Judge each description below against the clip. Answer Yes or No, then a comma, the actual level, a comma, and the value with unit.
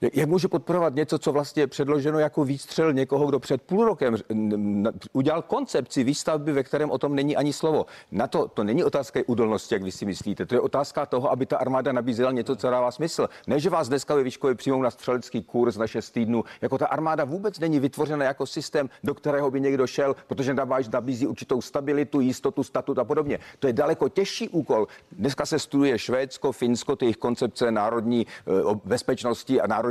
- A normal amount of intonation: Yes, average, 3.5 semitones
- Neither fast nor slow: No, fast, 195 wpm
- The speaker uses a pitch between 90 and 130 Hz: No, medium, 140 Hz